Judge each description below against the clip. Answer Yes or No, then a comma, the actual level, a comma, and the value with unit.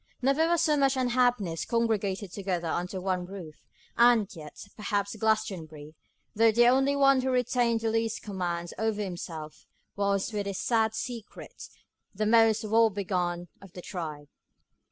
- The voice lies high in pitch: Yes, high, 210 Hz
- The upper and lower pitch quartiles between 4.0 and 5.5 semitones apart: Yes, average, 4.5 semitones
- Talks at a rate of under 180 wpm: Yes, average, 150 wpm